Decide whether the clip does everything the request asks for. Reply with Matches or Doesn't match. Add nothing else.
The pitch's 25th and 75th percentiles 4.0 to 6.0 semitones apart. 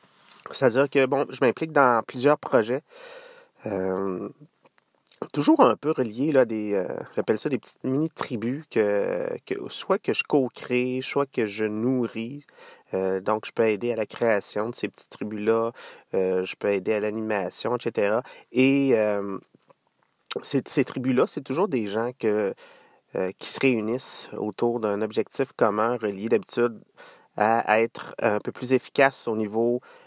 Matches